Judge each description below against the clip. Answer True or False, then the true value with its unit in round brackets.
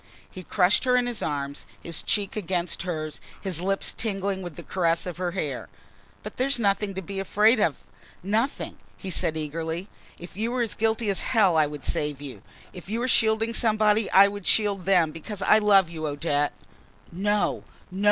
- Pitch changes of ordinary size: True (4.4 semitones)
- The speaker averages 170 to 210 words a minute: True (190 wpm)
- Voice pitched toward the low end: False (190 Hz)